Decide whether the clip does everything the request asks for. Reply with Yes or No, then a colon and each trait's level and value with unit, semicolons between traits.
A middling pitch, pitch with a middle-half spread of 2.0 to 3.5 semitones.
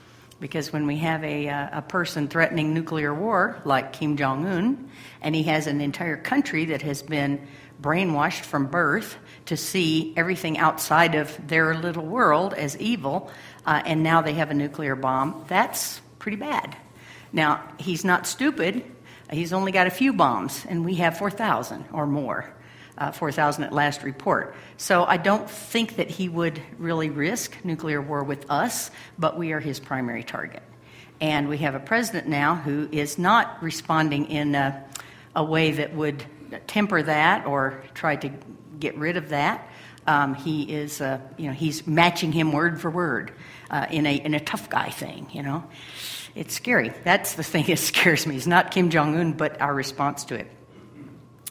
Yes: medium, 155 Hz; narrow, 2.6 semitones